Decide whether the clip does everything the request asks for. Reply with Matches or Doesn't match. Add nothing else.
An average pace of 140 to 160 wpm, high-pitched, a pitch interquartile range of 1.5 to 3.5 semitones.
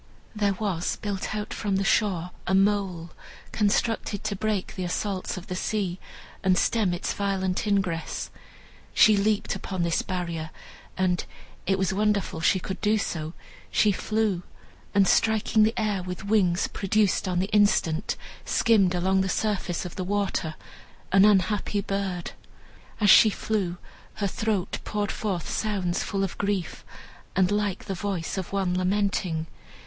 Matches